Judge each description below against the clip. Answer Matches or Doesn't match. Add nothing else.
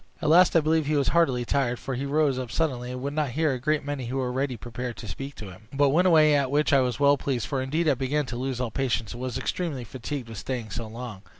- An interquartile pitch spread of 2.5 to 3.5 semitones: Matches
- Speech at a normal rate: Doesn't match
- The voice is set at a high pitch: Doesn't match